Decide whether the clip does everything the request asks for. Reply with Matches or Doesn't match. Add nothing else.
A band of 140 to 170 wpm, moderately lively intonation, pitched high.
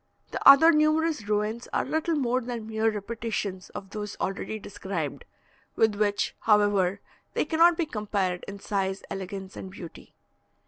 Matches